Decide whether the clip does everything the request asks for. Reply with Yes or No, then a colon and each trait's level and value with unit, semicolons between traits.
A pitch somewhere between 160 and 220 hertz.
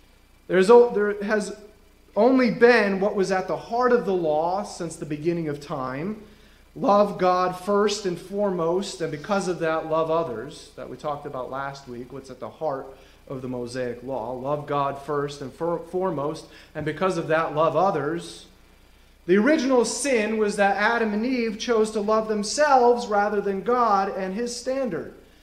Yes: medium, 185 Hz